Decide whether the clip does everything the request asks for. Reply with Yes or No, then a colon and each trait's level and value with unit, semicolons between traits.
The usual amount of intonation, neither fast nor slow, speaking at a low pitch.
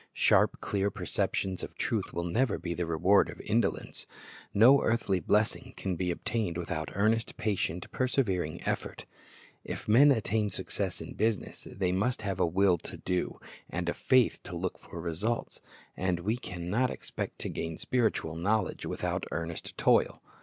Yes: average, 4.2 semitones; average, 160 wpm; very low, 95 Hz